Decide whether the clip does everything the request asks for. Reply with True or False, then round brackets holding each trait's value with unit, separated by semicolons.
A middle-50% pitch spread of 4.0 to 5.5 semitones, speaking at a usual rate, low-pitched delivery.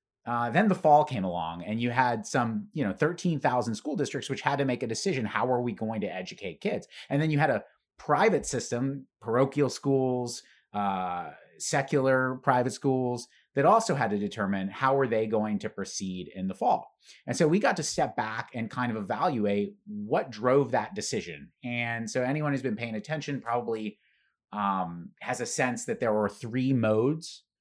True (4.5 semitones; 190 wpm; 120 Hz)